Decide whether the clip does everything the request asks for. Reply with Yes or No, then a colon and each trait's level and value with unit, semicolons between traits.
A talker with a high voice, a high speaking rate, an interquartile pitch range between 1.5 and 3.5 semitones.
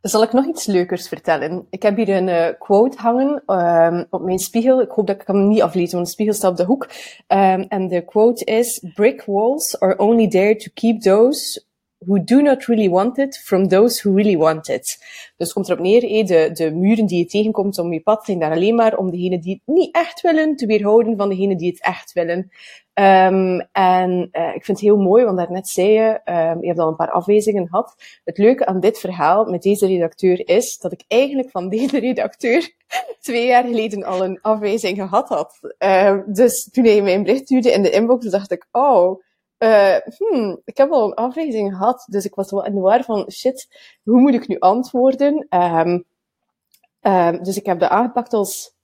No: high, 205 Hz; fast, 215 wpm; average, 4.4 semitones